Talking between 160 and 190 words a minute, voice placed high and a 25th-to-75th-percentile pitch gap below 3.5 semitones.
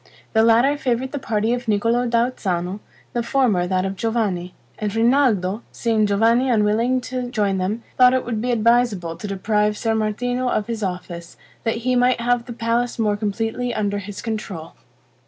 Yes: average, 175 wpm; high, 225 Hz; average, 3.1 semitones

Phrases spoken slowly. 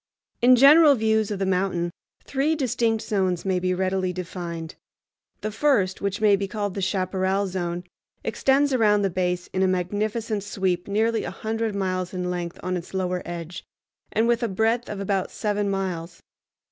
No: average, 170 wpm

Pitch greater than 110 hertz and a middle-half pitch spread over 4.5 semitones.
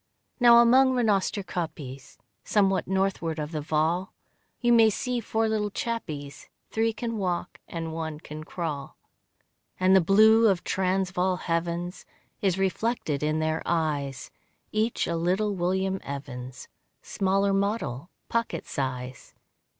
Yes: medium, 185 Hz; average, 5.1 semitones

